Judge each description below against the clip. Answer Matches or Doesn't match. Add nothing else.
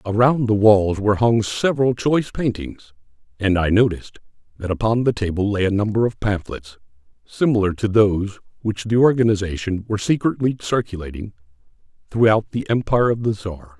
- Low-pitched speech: Matches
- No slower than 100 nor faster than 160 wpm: Matches